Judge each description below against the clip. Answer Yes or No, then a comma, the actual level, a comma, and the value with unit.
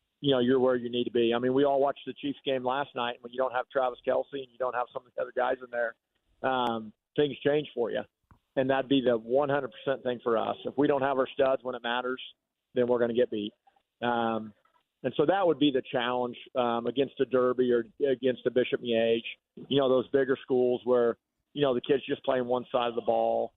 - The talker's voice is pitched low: Yes, low, 125 Hz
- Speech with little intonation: Yes, narrow, 2.0 semitones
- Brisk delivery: Yes, fast, 250 wpm